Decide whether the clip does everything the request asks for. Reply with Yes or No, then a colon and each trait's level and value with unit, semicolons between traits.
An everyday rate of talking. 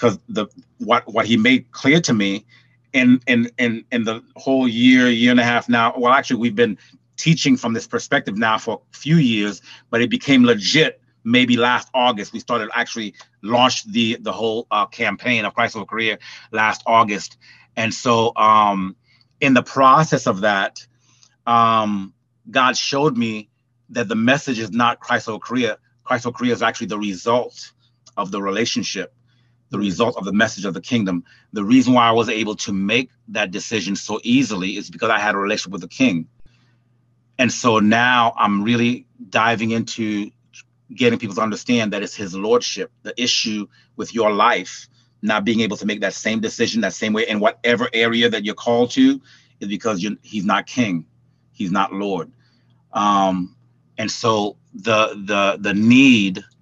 Yes: average, 180 wpm